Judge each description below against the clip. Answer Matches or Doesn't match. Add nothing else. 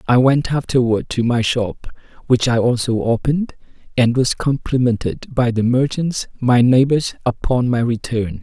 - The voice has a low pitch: Matches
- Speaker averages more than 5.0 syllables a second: Doesn't match